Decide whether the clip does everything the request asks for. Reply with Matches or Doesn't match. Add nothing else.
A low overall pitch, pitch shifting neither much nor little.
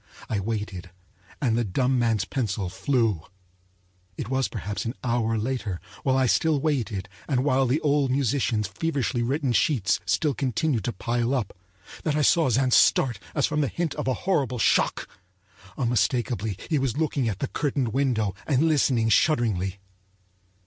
Matches